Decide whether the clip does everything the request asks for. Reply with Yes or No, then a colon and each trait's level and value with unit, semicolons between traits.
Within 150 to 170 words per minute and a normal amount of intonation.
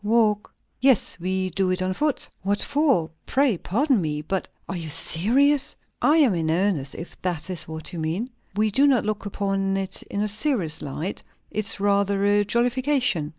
No: average, 180 wpm; average, 4.9 semitones